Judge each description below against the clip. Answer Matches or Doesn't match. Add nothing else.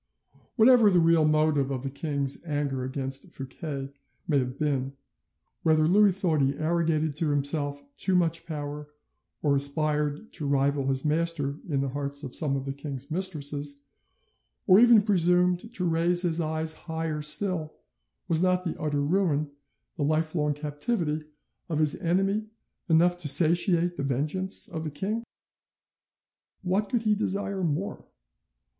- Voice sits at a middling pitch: Matches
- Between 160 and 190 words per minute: Doesn't match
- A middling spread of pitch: Matches